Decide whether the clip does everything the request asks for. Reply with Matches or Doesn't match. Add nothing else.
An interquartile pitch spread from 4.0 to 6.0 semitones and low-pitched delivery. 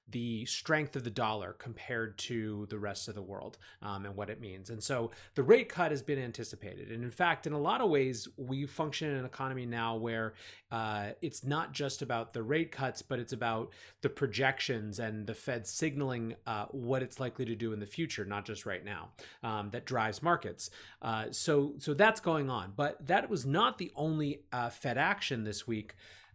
Matches